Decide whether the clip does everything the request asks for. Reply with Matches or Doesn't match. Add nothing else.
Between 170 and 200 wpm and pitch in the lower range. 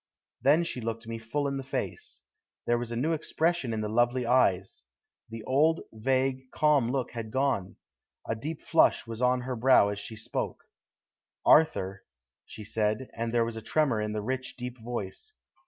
Matches